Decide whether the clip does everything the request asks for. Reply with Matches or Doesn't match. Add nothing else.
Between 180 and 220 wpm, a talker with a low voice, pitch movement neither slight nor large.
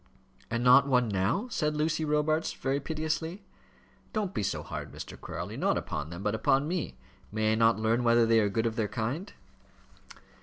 Doesn't match